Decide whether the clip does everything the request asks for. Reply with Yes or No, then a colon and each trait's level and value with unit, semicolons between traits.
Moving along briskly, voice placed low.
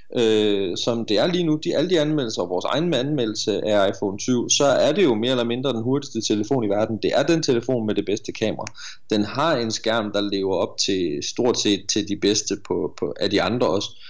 Yes: fast, 240 wpm; low, 115 Hz